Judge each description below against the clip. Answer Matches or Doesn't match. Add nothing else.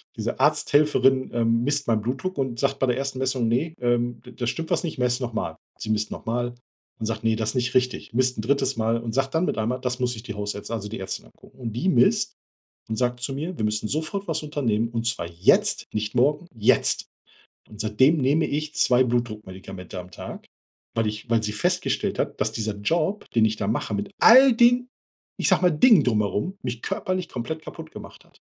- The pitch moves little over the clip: Doesn't match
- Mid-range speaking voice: Doesn't match